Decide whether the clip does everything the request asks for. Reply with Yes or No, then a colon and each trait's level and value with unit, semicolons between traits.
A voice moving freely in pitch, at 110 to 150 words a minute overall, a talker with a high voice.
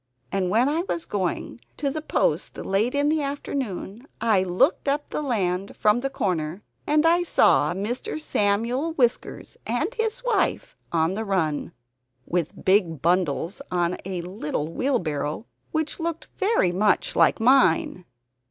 Yes: wide, 8.0 semitones; average, 145 wpm; high, 215 Hz